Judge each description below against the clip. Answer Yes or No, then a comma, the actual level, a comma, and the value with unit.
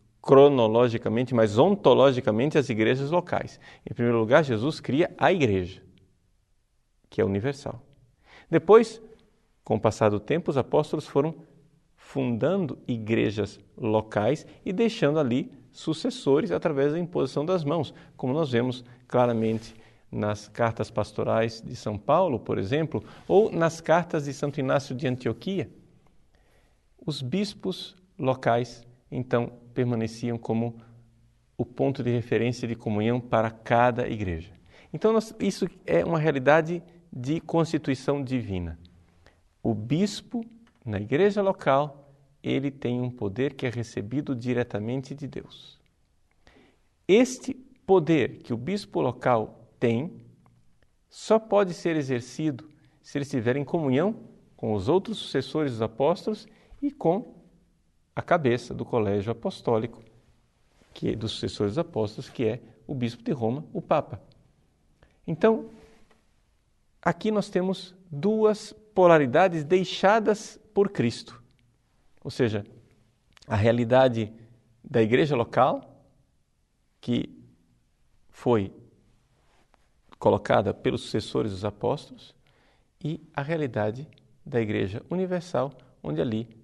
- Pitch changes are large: Yes, wide, 6.3 semitones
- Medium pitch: No, low, 130 Hz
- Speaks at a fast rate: No, slow, 120 wpm